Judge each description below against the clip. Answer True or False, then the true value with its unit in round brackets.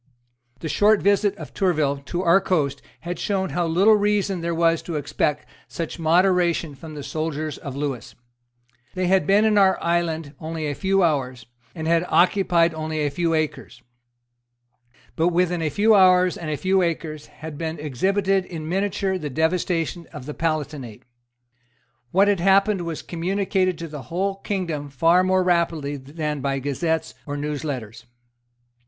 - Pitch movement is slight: False (3.8 semitones)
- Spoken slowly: False (160 wpm)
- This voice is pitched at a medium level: True (165 Hz)